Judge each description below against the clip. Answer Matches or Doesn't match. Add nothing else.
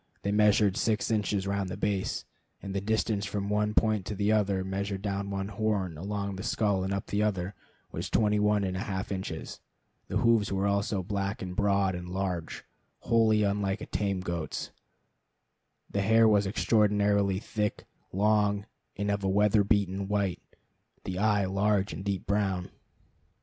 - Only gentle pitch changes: Matches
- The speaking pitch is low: Matches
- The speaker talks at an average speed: Matches